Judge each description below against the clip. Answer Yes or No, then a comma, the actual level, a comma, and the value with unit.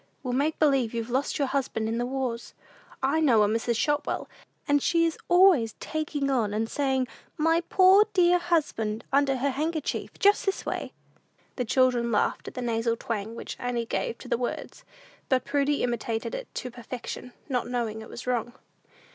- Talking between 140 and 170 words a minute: No, average, 180 wpm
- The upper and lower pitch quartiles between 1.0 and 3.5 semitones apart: No, average, 4.4 semitones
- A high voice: Yes, very high, 255 Hz